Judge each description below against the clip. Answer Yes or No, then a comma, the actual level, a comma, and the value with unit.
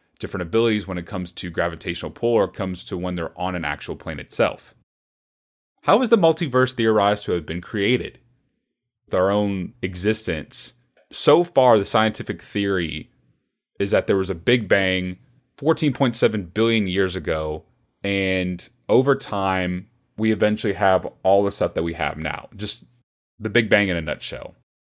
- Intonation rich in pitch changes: No, average, 4.0 semitones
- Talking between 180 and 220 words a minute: No, average, 160 wpm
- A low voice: Yes, low, 100 Hz